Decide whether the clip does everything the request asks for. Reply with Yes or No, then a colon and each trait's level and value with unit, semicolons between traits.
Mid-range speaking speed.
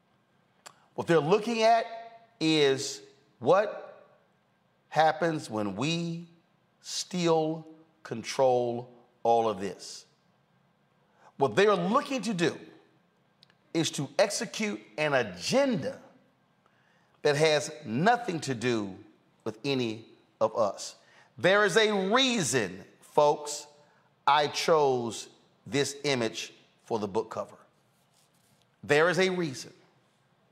No: slow, 100 wpm